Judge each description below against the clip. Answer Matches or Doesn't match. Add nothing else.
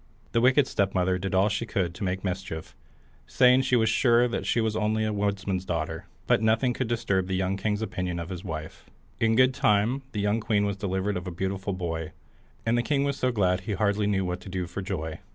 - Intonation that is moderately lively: Matches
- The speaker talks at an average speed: Doesn't match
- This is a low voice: Matches